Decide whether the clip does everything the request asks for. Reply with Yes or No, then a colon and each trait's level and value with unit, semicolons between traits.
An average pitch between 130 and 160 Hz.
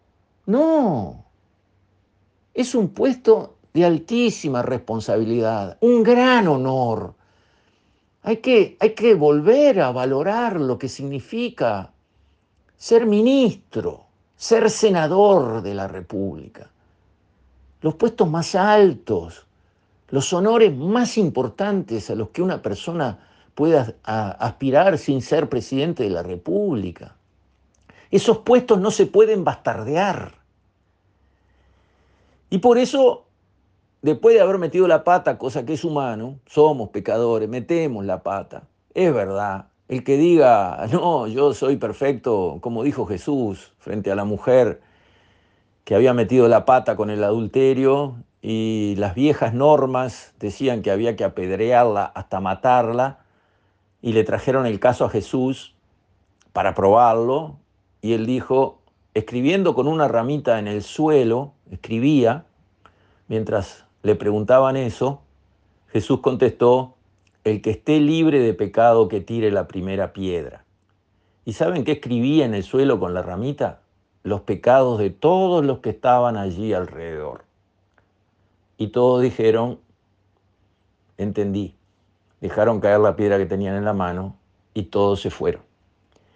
No: low, 115 Hz